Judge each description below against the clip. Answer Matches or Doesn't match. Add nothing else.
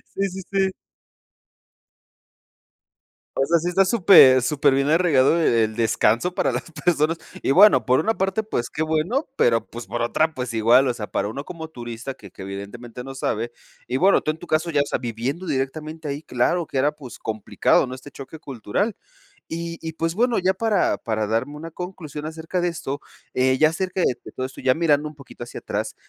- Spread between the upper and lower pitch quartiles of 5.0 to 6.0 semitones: Matches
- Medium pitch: Matches